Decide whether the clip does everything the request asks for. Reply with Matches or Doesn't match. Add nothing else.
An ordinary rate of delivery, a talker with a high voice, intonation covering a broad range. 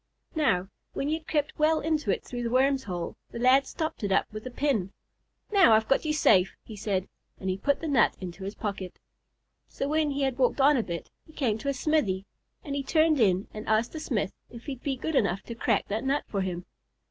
Doesn't match